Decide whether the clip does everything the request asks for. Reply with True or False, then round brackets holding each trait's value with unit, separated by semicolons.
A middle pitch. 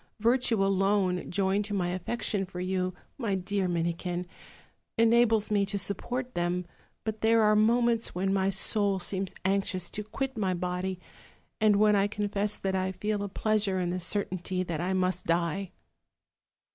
False (195 Hz)